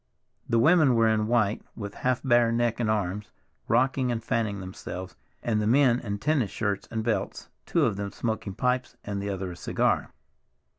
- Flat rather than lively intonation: No, average, 3.0 semitones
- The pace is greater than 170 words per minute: Yes, average, 185 wpm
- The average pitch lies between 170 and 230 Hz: No, low, 110 Hz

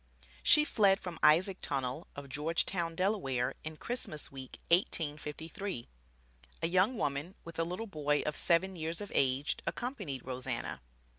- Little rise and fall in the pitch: No, average, 5.0 semitones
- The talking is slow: No, average, 145 wpm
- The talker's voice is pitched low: No, medium, 165 Hz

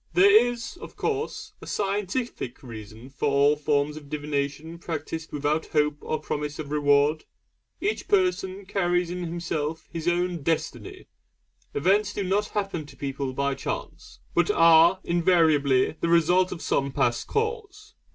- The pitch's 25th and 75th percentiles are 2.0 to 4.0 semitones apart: No, average, 4.9 semitones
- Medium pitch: Yes, medium, 165 Hz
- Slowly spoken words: No, average, 145 wpm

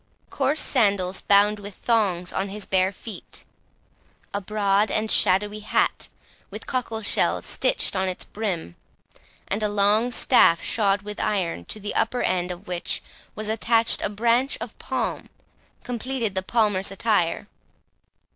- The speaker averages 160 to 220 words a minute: No, average, 145 wpm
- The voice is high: Yes, high, 205 Hz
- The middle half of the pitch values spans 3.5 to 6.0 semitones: No, average, 2.7 semitones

